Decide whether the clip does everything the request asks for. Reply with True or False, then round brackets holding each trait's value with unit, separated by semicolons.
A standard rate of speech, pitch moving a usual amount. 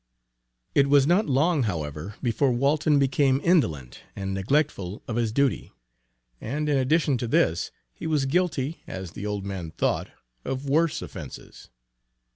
False (145 wpm; 6.9 semitones)